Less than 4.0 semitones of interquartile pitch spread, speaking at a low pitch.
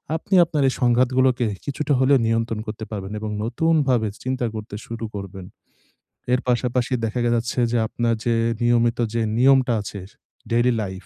Yes: narrow, 2.4 semitones; low, 120 Hz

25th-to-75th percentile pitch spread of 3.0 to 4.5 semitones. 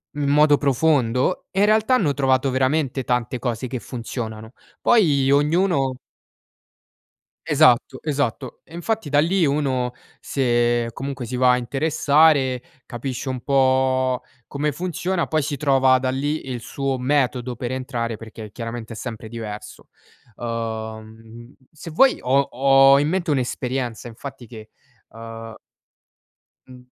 Yes: average, 3.3 semitones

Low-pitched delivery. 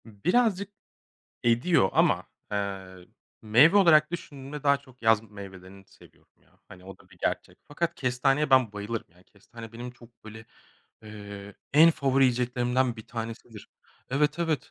Yes: low, 120 Hz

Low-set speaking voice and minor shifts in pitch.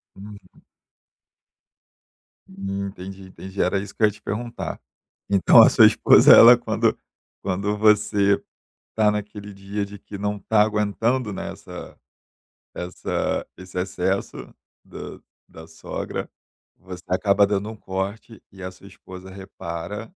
Yes: low, 100 Hz; narrow, 1.8 semitones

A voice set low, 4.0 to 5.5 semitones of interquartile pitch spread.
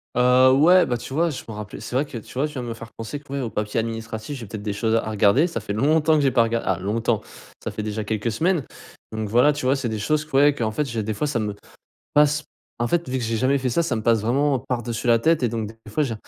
Yes: low, 120 Hz; average, 4.5 semitones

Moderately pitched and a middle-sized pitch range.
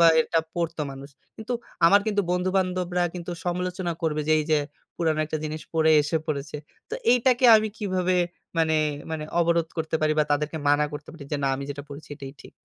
Yes: medium, 165 Hz; average, 3.0 semitones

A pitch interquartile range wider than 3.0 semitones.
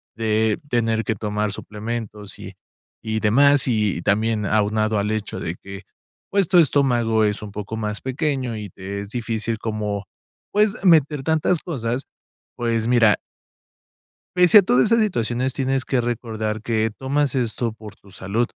Yes: average, 3.7 semitones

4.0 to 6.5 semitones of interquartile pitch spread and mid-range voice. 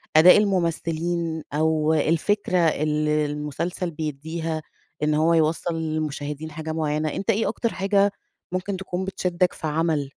No: average, 2.7 semitones; medium, 160 Hz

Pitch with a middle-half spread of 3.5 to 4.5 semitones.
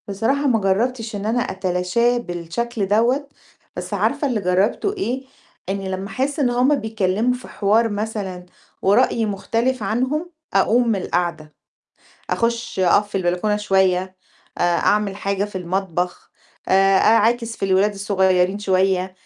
Yes: average, 3.8 semitones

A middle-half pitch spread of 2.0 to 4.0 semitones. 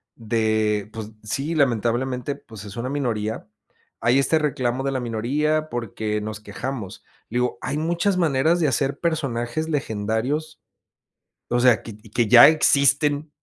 No: average, 4.7 semitones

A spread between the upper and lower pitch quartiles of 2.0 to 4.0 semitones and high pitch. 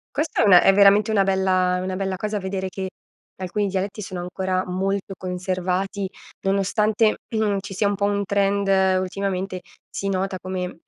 No: narrow, 1.3 semitones; high, 195 Hz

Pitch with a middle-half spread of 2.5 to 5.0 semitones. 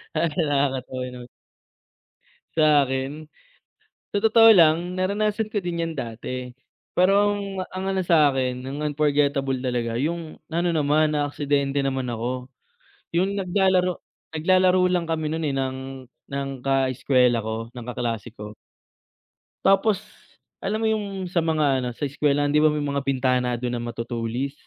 No: wide, 5.4 semitones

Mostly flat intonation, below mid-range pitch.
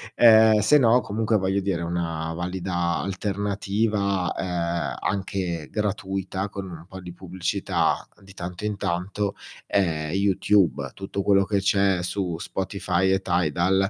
Yes: narrow, 2.3 semitones; very low, 95 Hz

